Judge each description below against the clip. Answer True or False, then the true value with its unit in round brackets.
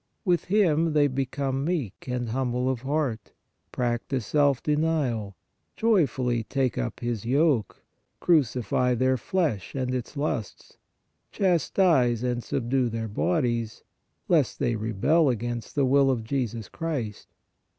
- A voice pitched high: False (130 Hz)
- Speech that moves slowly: True (130 wpm)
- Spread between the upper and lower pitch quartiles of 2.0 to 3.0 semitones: False (4.1 semitones)